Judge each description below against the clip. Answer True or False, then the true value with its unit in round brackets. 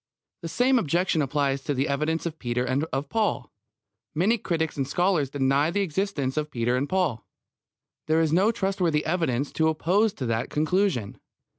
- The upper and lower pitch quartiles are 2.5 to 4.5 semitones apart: False (5.0 semitones)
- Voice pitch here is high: False (155 Hz)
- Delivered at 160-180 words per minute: True (170 wpm)